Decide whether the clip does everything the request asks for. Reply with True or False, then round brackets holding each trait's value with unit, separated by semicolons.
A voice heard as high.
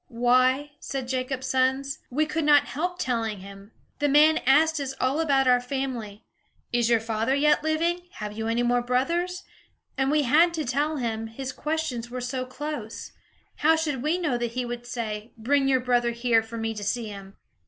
True (255 Hz)